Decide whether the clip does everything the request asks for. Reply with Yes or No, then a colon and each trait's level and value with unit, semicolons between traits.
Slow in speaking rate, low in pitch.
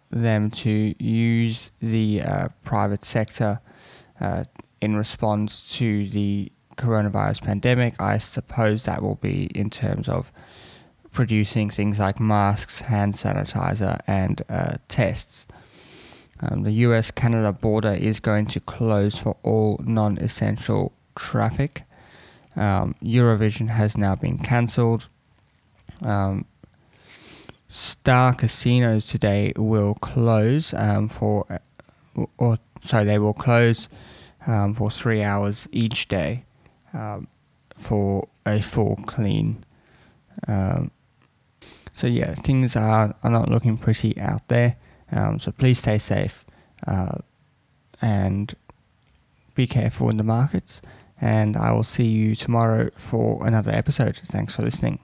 Yes: slow, 120 wpm; low, 110 Hz